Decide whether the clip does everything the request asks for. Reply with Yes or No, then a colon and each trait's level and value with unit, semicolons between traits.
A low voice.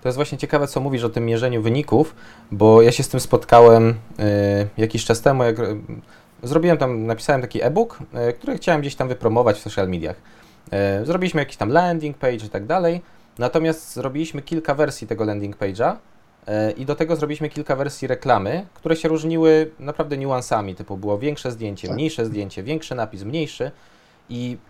Yes: low, 125 Hz